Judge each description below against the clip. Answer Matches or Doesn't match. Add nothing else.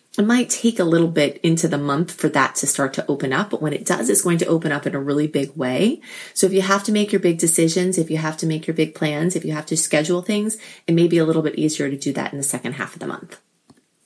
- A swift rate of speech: Matches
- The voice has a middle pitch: Matches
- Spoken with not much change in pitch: Doesn't match